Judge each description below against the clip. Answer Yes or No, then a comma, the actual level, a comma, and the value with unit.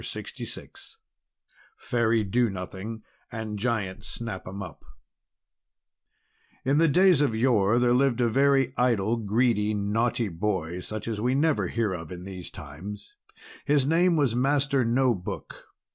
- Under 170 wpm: Yes, average, 145 wpm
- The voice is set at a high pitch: No, low, 115 Hz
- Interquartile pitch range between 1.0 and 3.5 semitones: No, average, 4.4 semitones